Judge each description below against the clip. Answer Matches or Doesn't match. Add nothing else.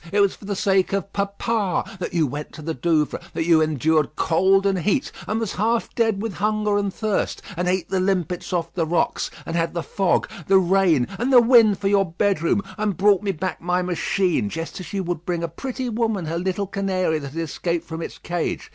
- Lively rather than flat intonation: Doesn't match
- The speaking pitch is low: Doesn't match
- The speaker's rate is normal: Doesn't match